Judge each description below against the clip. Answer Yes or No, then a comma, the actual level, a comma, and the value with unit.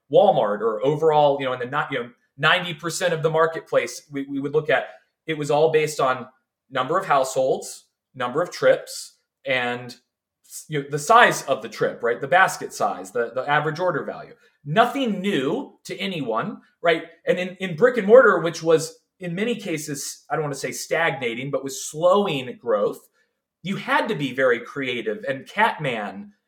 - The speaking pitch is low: No, medium, 165 Hz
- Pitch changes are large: Yes, wide, 8.3 semitones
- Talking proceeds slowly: No, average, 185 wpm